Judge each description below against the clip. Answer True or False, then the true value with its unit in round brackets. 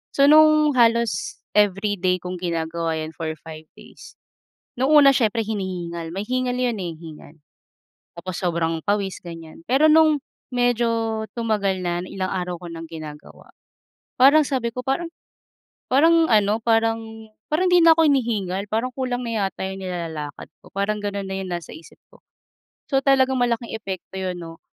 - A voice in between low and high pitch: False (205 Hz)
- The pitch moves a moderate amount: False (6.4 semitones)